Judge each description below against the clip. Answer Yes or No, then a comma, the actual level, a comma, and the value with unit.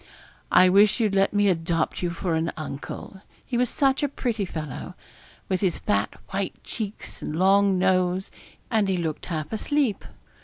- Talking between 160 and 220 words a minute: Yes, average, 165 wpm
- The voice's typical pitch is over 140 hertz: Yes, high, 190 Hz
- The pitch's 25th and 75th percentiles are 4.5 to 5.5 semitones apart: No, average, 3.4 semitones